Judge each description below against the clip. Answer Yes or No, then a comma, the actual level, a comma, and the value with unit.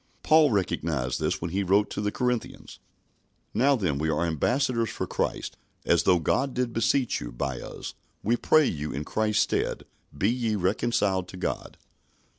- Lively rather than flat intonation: Yes, wide, 6.2 semitones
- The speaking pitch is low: Yes, low, 105 Hz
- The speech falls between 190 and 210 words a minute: No, average, 170 wpm